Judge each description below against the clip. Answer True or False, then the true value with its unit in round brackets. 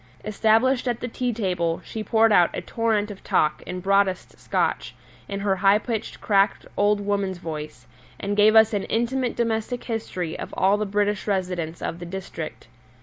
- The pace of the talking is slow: False (175 wpm)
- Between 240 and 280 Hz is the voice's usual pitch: False (205 Hz)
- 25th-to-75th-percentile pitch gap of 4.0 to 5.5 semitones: False (3.1 semitones)